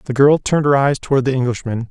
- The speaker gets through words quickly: Yes, fast, 250 wpm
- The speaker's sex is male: Yes, male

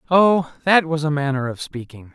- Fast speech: No, average, 195 wpm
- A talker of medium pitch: Yes, medium, 150 Hz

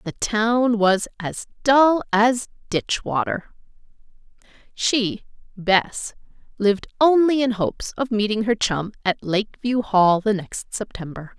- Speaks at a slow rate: Yes, slow, 125 wpm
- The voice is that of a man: No, female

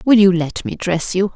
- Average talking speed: No, fast, 265 wpm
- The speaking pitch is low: No, medium, 185 Hz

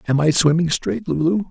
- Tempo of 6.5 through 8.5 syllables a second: No, 5.2 syllables/s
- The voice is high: No, medium, 165 Hz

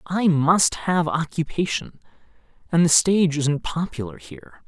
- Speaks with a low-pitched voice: No, medium, 150 Hz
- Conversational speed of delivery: No, slow, 130 wpm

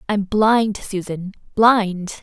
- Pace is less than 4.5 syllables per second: Yes, 2.7 syllables/s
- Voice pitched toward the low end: No, high, 205 Hz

